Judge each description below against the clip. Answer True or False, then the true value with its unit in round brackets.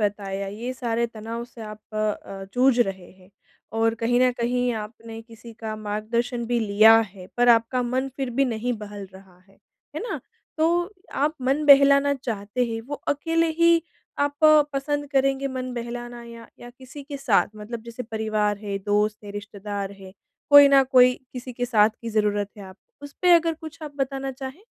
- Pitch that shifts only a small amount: False (4.2 semitones)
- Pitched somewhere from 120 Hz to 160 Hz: False (235 Hz)